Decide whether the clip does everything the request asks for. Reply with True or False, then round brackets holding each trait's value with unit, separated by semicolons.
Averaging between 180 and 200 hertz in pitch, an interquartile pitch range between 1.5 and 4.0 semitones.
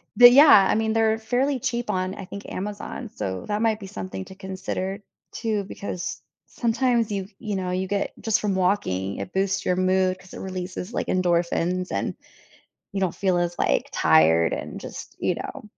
True (190 Hz; 2.9 semitones)